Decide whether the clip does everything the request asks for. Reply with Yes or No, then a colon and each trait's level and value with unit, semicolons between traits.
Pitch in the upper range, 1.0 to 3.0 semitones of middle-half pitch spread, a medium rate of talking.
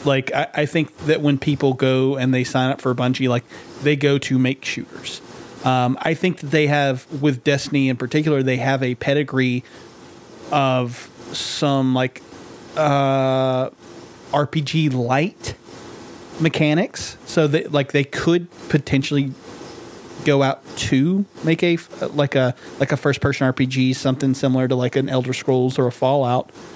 No: low, 135 Hz; narrow, 2.5 semitones; average, 155 wpm